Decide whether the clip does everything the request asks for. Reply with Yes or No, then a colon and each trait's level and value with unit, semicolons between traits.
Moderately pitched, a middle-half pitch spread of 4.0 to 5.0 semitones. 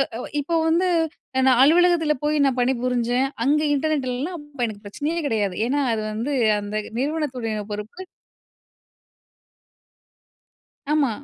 No: very high, 270 Hz; average, 4.3 semitones